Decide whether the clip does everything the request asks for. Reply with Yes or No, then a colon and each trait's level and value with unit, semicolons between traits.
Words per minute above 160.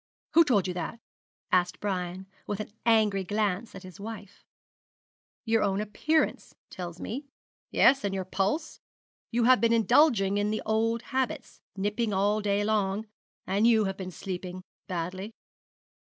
No: average, 150 wpm